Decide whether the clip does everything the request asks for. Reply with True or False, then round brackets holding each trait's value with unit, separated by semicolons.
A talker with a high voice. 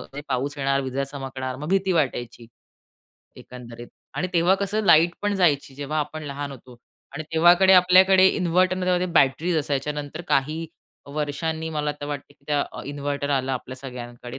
False (145 Hz)